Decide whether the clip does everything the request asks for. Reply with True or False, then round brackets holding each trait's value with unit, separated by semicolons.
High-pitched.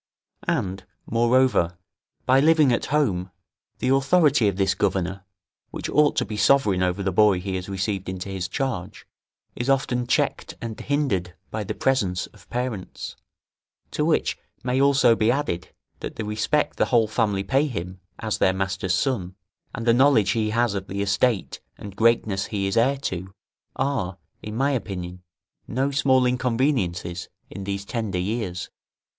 False (110 Hz)